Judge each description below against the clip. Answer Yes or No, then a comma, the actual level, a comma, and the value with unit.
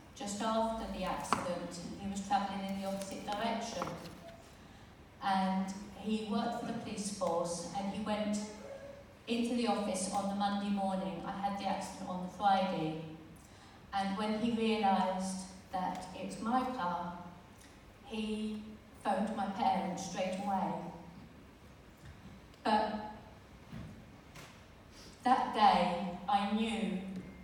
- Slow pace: Yes, slow, 120 wpm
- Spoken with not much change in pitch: Yes, narrow, 2.3 semitones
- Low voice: No, high, 200 Hz